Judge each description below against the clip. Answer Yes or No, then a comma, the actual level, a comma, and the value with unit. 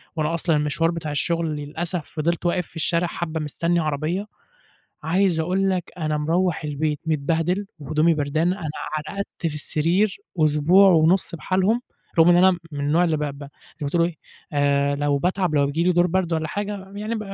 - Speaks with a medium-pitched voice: Yes, medium, 165 Hz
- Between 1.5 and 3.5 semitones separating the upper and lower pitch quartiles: Yes, average, 3.0 semitones